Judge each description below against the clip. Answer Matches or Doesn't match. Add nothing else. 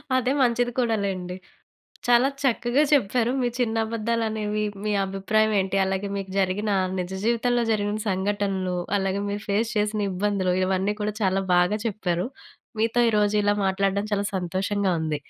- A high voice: Matches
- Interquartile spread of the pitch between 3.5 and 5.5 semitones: Doesn't match